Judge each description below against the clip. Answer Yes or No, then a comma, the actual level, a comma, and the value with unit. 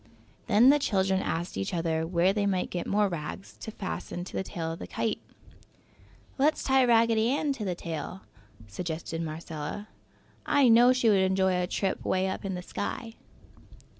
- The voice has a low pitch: No, high, 190 Hz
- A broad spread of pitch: No, average, 4.7 semitones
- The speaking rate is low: No, average, 175 wpm